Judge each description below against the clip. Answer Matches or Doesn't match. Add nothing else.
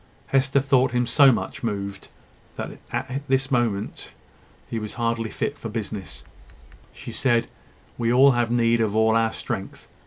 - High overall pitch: Doesn't match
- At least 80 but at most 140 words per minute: Doesn't match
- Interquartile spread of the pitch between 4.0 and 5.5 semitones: Doesn't match